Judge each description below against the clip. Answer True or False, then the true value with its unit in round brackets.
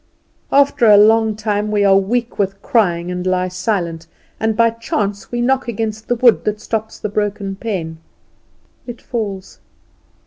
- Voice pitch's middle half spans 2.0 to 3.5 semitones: True (2.9 semitones)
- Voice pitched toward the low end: False (210 Hz)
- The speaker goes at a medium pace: True (160 wpm)